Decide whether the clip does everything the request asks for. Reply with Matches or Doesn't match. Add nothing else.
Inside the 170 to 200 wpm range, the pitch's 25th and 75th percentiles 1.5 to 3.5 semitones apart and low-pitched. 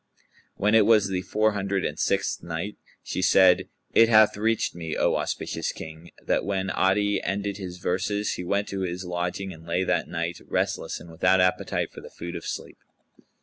Matches